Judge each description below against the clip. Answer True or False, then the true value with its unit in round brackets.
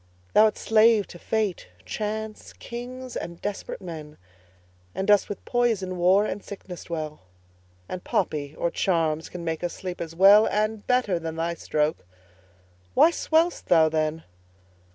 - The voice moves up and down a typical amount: True (4.7 semitones)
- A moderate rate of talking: True (145 wpm)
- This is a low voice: False (185 Hz)